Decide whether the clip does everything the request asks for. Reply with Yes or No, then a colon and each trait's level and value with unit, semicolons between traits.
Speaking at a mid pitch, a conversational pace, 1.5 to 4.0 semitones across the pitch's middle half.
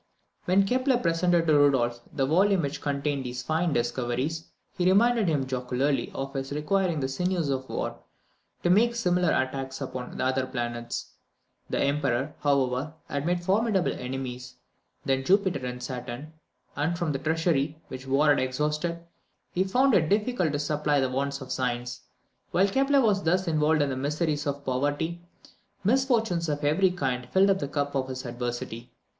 No: medium, 145 Hz; average, 165 wpm; average, 5.2 semitones